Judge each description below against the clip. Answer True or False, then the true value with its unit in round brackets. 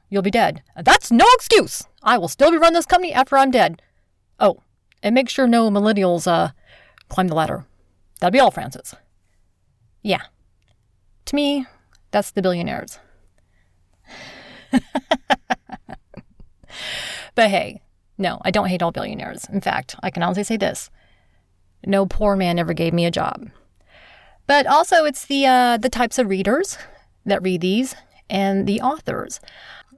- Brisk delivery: False (150 wpm)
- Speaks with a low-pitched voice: False (195 Hz)